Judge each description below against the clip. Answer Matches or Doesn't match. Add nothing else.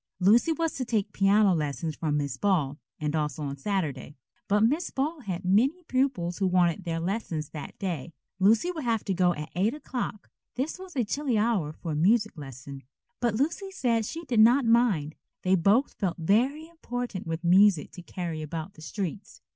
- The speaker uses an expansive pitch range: Matches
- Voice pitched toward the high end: Matches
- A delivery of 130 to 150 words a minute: Doesn't match